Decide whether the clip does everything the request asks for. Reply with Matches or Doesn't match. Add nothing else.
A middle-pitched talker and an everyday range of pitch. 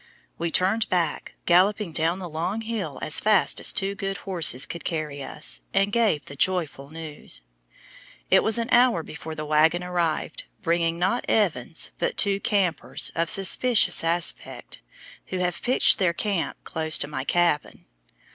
Matches